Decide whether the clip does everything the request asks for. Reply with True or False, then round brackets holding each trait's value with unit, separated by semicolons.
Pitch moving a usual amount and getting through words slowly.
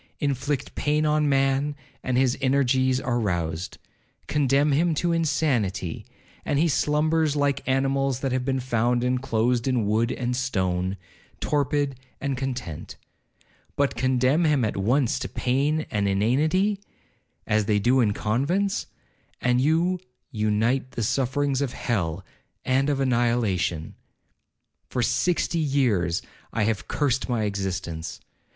True (4.2 semitones; 130 wpm)